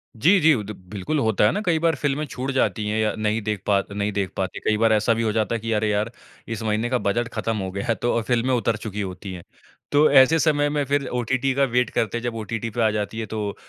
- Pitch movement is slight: No, average, 3.7 semitones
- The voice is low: Yes, low, 115 Hz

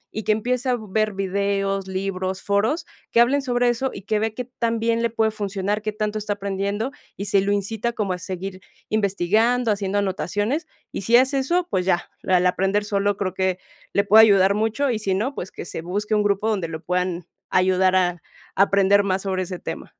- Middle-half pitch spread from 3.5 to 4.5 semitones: No, average, 2.7 semitones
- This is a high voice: Yes, high, 200 Hz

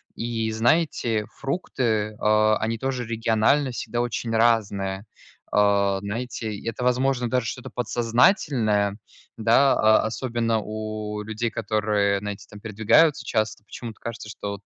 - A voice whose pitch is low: Yes, low, 110 Hz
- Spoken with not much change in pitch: Yes, narrow, 2.2 semitones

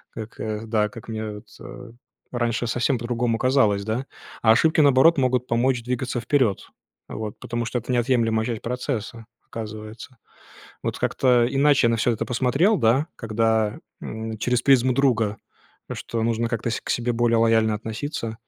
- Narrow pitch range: Yes, narrow, 2.2 semitones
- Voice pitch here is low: Yes, low, 115 Hz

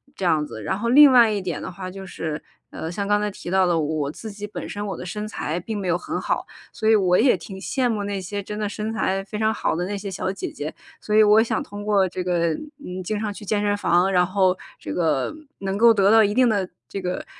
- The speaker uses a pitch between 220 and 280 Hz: No, high, 195 Hz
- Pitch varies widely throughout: No, average, 2.8 semitones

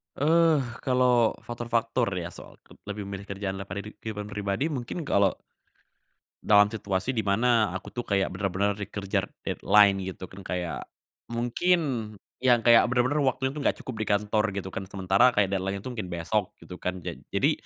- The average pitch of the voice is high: No, low, 105 Hz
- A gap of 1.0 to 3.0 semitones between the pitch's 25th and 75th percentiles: No, average, 3.8 semitones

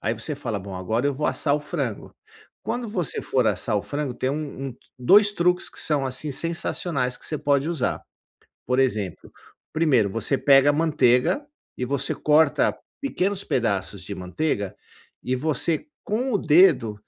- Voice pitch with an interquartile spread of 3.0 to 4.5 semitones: No, average, 5.0 semitones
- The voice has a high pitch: No, medium, 140 Hz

